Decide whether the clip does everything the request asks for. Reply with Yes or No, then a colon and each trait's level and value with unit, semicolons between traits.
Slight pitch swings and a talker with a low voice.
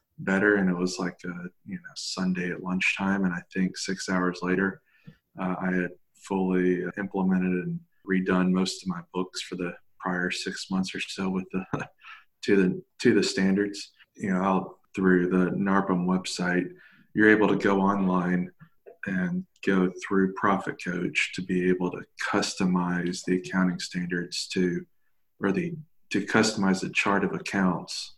Yes: narrow, 1.2 semitones; very low, 95 Hz